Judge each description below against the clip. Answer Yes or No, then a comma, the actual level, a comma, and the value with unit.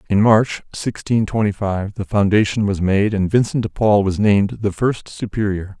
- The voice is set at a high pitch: No, low, 105 Hz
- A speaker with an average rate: Yes, average, 185 wpm